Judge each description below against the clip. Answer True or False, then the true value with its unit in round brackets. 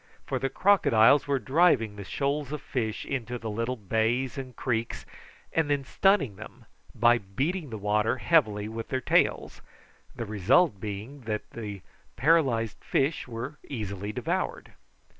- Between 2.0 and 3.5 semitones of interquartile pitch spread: False (4.5 semitones)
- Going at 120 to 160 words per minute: True (145 wpm)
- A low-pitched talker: True (120 Hz)